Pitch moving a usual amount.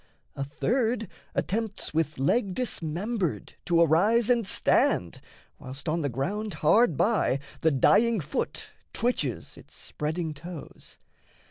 No: wide, 6.8 semitones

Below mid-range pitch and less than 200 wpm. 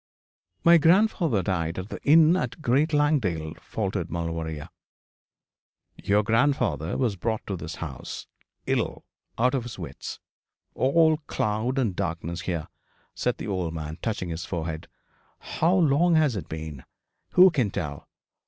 Yes: low, 100 Hz; average, 140 wpm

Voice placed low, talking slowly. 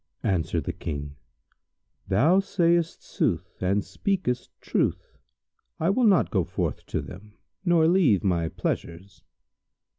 Yes: low, 105 Hz; slow, 120 wpm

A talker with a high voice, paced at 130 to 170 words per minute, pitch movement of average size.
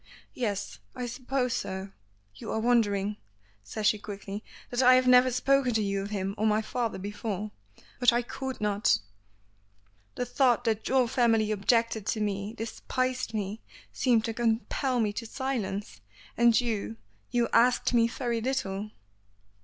Yes: high, 225 Hz; average, 155 wpm; average, 3.2 semitones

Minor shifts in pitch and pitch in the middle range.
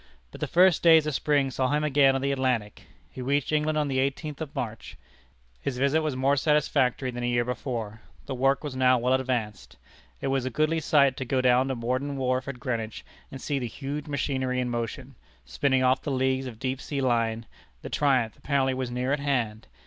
No: narrow, 2.1 semitones; low, 130 Hz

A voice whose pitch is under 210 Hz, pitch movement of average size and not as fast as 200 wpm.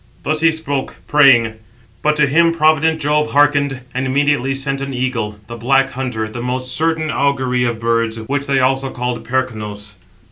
Yes: low, 135 Hz; average, 3.0 semitones; average, 170 wpm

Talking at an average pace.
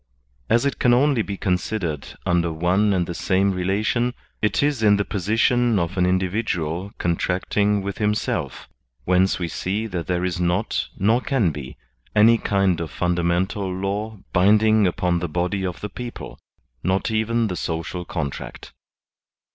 Yes: average, 155 wpm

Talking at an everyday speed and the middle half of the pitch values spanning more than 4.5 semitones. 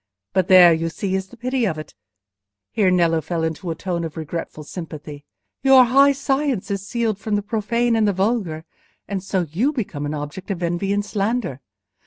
Yes: average, 185 wpm; wide, 5.5 semitones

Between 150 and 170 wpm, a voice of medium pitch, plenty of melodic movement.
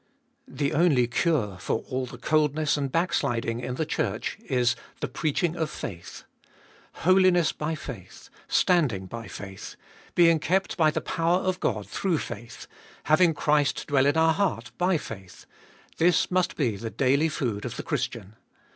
Yes: average, 160 wpm; medium, 150 Hz; wide, 5.7 semitones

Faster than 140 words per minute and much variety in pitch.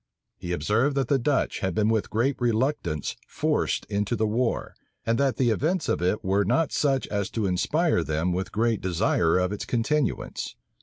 Yes: average, 185 wpm; wide, 6.0 semitones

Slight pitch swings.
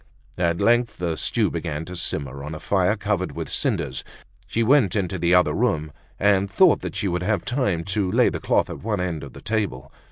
No: average, 4.1 semitones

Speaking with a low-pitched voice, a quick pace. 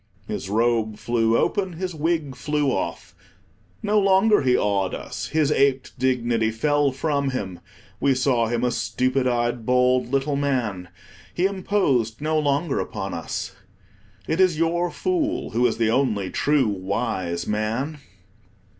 No: low, 130 Hz; average, 145 wpm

